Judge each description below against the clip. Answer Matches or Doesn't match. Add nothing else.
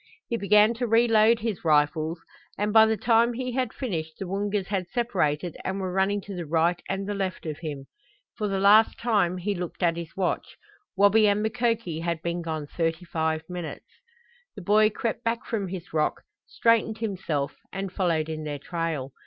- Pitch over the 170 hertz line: Matches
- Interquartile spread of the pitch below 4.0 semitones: Doesn't match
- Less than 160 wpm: Doesn't match